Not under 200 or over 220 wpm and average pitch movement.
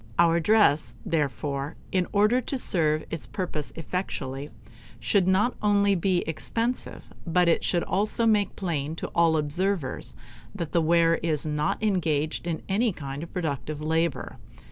No: average, 145 wpm; average, 4.2 semitones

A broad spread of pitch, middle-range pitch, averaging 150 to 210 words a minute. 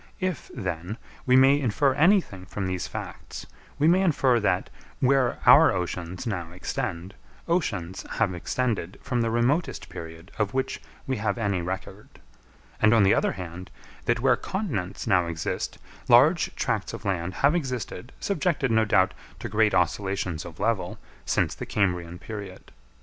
No: wide, 6.3 semitones; low, 105 Hz; average, 155 wpm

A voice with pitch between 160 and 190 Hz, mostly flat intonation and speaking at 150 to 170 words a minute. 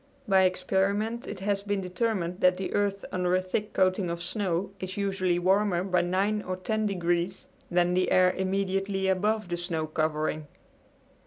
Yes: medium, 185 Hz; narrow, 2.0 semitones; average, 165 wpm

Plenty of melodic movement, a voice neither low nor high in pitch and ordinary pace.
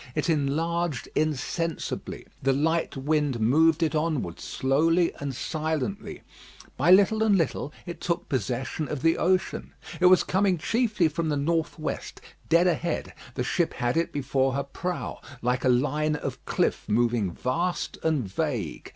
No: average, 4.0 semitones; medium, 155 Hz; average, 150 wpm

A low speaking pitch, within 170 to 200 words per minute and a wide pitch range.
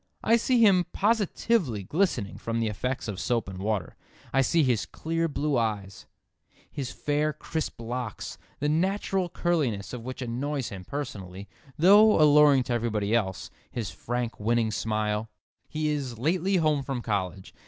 No: low, 125 Hz; average, 155 wpm; wide, 6.3 semitones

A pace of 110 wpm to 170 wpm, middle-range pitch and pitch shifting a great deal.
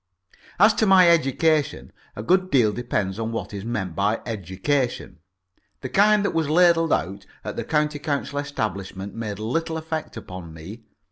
No: average, 160 wpm; low, 125 Hz; wide, 8.0 semitones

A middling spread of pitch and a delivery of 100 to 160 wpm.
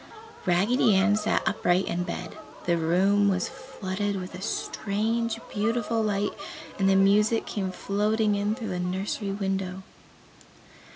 No: narrow, 2.3 semitones; slow, 135 wpm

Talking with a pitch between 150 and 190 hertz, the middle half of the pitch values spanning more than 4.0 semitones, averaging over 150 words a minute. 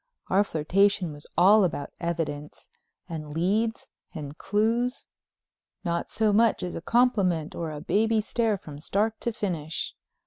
No: medium, 185 Hz; wide, 5.5 semitones; slow, 135 wpm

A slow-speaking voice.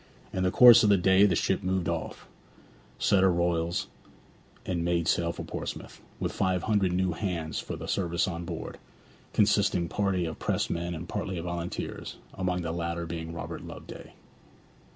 No: average, 170 wpm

